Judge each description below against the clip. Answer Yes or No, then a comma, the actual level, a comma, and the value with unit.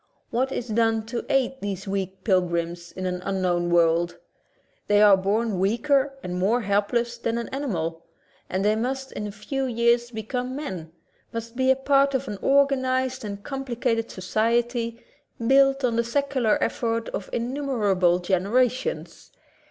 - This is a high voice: Yes, high, 230 Hz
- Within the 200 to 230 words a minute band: No, average, 155 wpm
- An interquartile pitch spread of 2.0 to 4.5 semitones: No, average, 5.0 semitones